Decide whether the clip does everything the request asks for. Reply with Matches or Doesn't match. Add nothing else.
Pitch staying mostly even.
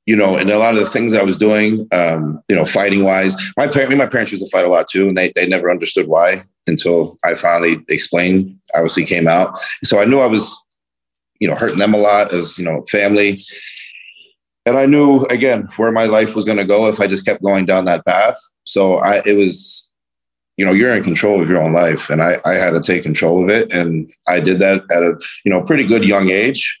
Doesn't match